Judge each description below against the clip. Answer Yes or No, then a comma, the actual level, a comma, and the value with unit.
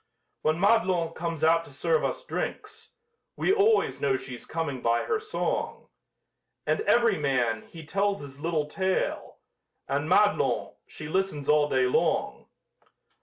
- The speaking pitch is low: No, medium, 165 Hz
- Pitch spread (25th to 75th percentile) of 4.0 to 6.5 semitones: Yes, wide, 5.6 semitones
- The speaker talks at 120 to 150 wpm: Yes, average, 140 wpm